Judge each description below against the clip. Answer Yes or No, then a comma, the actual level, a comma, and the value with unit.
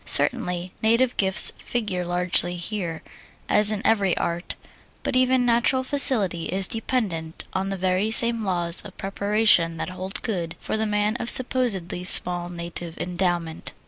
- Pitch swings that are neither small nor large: Yes, average, 4.1 semitones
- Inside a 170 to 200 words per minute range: No, average, 145 wpm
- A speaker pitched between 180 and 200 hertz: Yes, high, 190 Hz